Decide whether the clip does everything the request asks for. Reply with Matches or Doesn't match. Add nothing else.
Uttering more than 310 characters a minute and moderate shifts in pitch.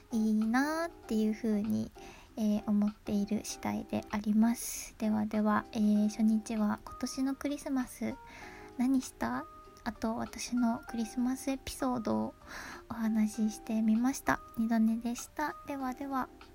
Doesn't match